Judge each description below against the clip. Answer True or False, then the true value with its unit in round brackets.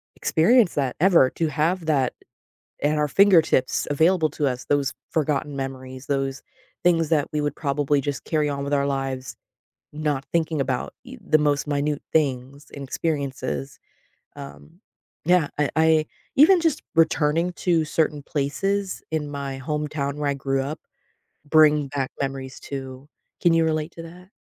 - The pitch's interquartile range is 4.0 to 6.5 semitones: False (2.8 semitones)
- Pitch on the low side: False (150 Hz)